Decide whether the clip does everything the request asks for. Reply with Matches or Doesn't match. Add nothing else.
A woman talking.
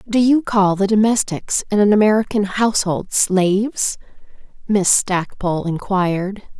Matches